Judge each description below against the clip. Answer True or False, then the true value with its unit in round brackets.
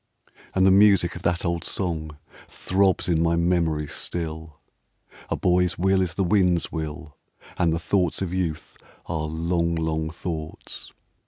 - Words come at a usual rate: True (150 wpm)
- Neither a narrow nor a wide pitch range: False (2.2 semitones)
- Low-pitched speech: True (85 Hz)